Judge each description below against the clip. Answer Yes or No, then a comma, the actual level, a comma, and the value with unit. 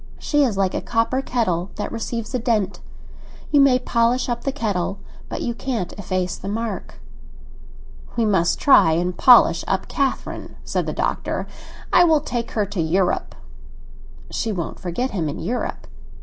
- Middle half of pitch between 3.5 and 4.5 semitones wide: No, average, 5.0 semitones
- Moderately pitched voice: No, high, 220 Hz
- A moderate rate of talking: Yes, average, 165 wpm